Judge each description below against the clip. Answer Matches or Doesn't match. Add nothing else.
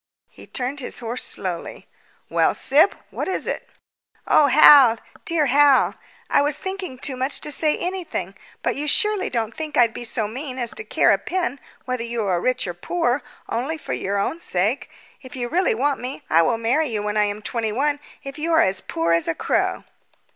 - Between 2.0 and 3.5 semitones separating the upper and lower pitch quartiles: Doesn't match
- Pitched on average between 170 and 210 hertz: Doesn't match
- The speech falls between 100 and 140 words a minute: Doesn't match